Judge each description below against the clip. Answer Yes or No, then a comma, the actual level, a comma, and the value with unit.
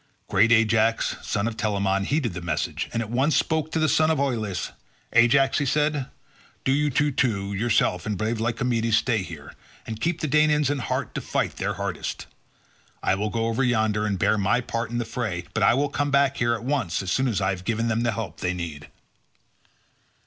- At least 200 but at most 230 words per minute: Yes, fast, 205 wpm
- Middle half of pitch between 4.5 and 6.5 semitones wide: Yes, average, 4.9 semitones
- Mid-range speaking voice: No, low, 115 Hz